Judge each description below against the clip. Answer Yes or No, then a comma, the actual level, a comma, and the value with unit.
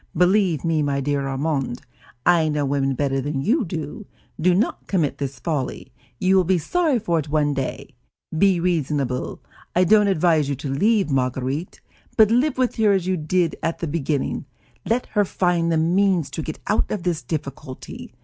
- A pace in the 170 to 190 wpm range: Yes, average, 180 wpm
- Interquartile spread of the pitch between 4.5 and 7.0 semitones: Yes, average, 4.9 semitones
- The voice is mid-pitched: Yes, medium, 165 Hz